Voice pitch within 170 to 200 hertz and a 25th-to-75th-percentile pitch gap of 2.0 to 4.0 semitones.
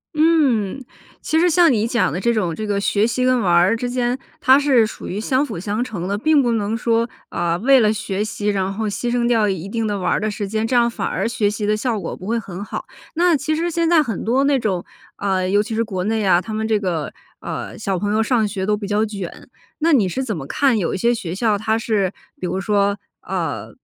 No: high, 215 Hz; average, 3.5 semitones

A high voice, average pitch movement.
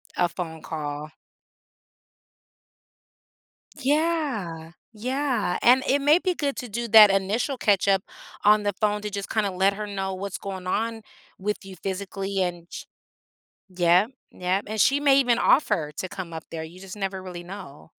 Yes: high, 195 Hz; average, 4.0 semitones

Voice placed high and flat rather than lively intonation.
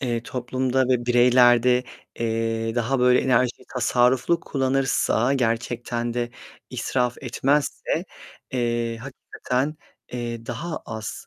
No: low, 125 Hz; narrow, 1.7 semitones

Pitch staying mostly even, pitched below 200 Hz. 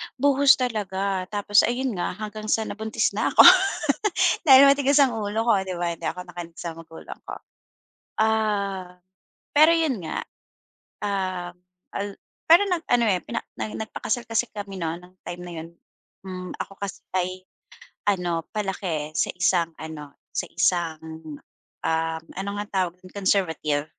No: average, 3.8 semitones; high, 190 Hz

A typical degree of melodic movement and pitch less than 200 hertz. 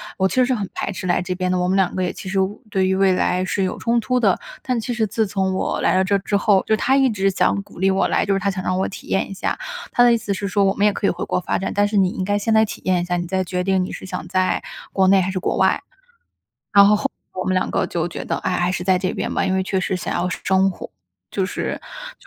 No: narrow, 1.7 semitones; high, 190 Hz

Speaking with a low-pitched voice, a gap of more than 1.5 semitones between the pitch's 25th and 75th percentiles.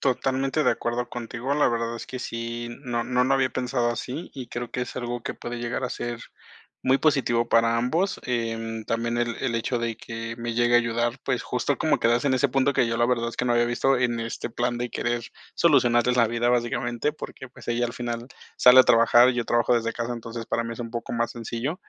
No: low, 120 Hz; narrow, 1.2 semitones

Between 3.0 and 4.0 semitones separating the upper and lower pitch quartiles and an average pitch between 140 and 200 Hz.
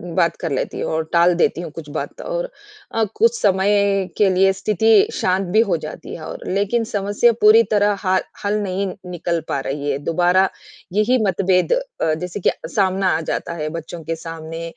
Yes: average, 3.6 semitones; medium, 185 Hz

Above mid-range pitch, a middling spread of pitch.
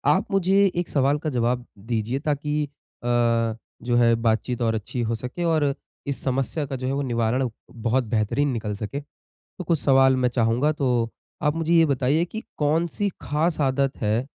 No: low, 135 Hz; average, 4.0 semitones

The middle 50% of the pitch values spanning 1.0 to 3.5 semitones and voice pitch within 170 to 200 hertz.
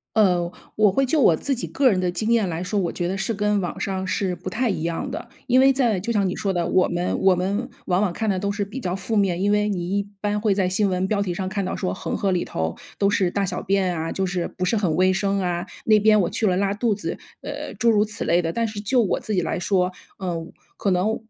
Yes: narrow, 2.6 semitones; high, 195 Hz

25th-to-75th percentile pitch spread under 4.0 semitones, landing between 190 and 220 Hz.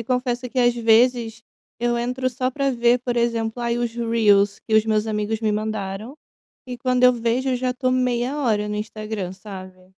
No: narrow, 2.6 semitones; high, 235 Hz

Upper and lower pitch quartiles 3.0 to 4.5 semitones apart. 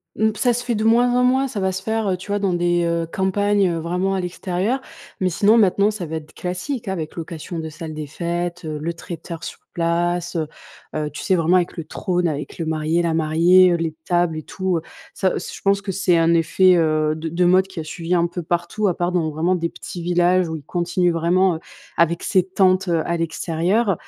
No: narrow, 2.4 semitones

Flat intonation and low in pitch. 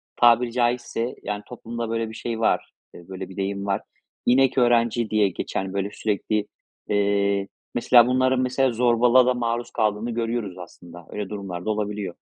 No: average, 3.1 semitones; low, 115 Hz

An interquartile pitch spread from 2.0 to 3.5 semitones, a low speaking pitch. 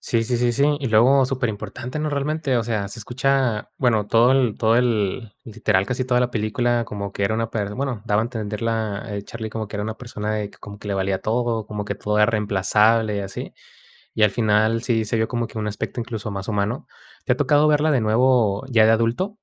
Yes: average, 2.7 semitones; low, 110 Hz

